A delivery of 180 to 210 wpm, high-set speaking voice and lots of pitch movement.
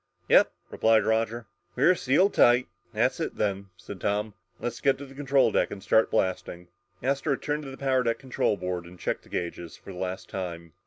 No: average, 200 wpm; low, 110 Hz; wide, 6.4 semitones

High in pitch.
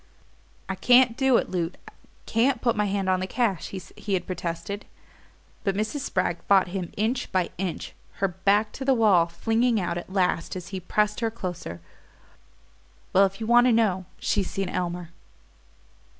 Yes: high, 195 Hz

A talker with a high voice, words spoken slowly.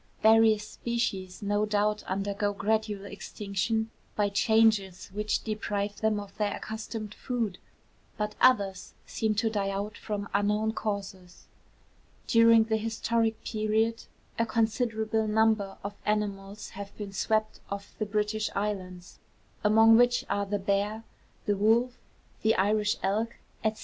Yes: high, 210 Hz; slow, 130 wpm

